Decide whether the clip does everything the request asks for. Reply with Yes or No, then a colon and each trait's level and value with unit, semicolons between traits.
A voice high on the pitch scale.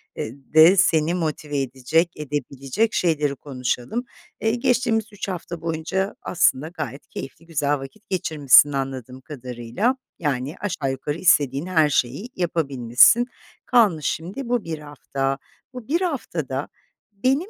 No: medium, 155 Hz